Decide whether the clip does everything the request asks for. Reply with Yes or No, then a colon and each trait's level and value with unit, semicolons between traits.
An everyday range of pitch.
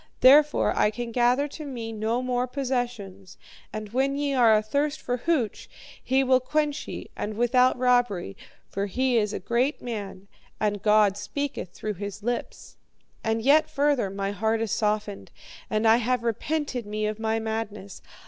Yes: average, 3.4 semitones